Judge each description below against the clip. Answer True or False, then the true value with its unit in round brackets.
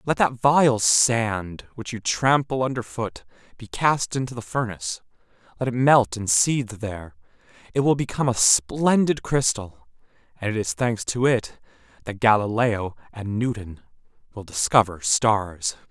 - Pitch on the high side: False (115 Hz)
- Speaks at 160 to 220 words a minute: False (145 wpm)